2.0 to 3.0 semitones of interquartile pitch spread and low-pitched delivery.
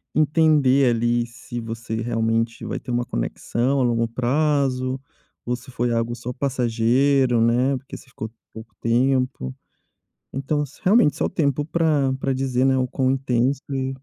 Yes: narrow, 2.6 semitones; low, 125 Hz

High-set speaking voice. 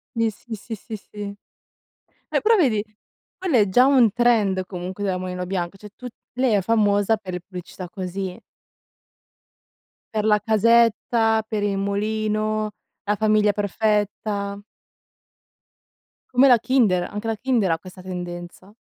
Yes: high, 210 Hz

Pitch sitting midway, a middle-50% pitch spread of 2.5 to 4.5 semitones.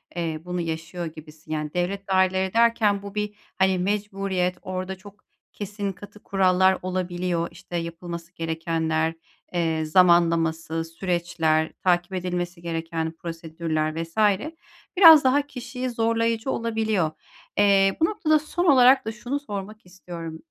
Yes: medium, 180 Hz; average, 3.8 semitones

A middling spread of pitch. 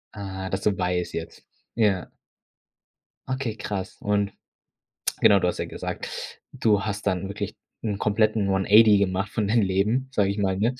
No: narrow, 1.9 semitones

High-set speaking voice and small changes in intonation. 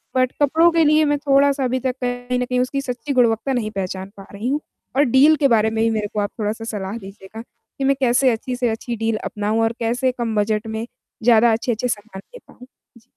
No: high, 235 Hz; average, 3.0 semitones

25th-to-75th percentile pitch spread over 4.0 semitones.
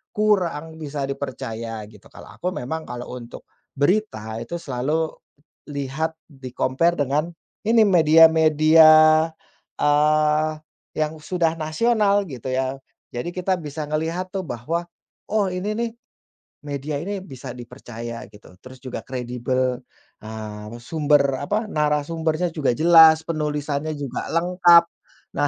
Yes: average, 4.4 semitones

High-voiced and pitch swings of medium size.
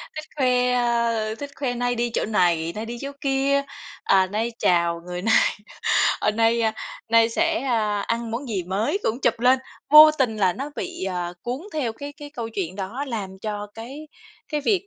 Yes: high, 230 Hz; average, 4.5 semitones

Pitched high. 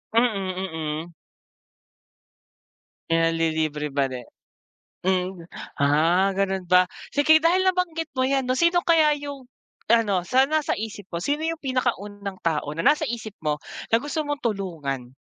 Yes: high, 200 Hz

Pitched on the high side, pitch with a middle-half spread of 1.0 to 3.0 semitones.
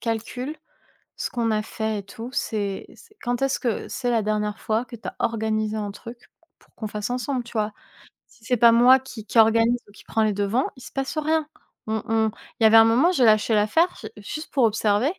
Yes: high, 225 Hz; narrow, 2.5 semitones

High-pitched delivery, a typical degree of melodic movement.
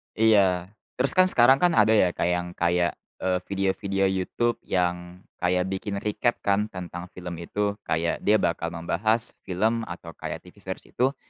No: very low, 95 Hz; average, 3.6 semitones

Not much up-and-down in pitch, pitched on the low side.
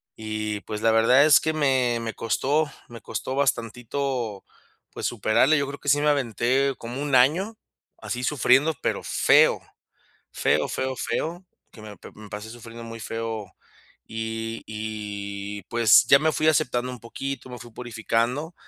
No: average, 3.7 semitones; low, 120 Hz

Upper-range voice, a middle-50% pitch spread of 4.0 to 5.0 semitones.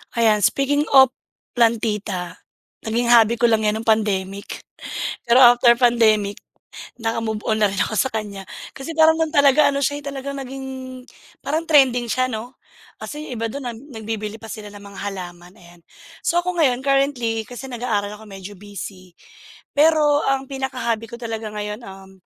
Yes: high, 230 Hz; average, 4.4 semitones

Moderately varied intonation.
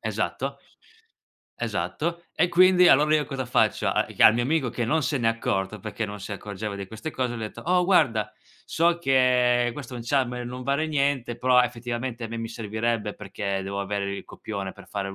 Yes: average, 4.5 semitones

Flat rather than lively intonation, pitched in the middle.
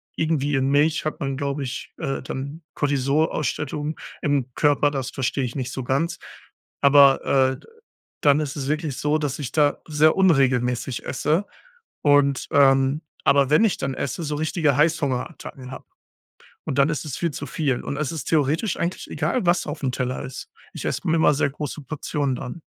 Yes: narrow, 2.3 semitones; medium, 145 Hz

